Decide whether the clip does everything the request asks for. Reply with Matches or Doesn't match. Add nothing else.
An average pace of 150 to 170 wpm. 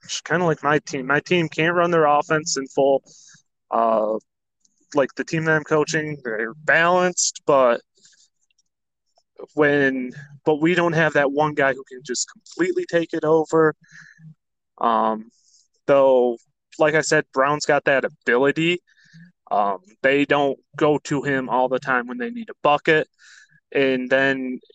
Matches